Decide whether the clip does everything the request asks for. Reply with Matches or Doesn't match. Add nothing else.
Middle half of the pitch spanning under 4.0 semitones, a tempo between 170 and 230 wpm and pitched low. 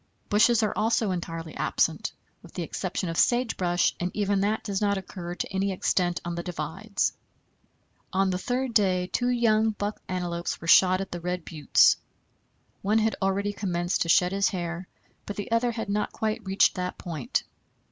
Doesn't match